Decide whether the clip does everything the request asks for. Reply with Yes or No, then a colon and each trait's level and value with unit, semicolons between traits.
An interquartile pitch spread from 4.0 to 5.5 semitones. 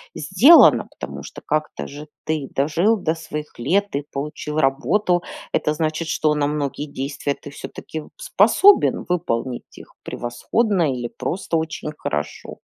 No: average, 3.4 semitones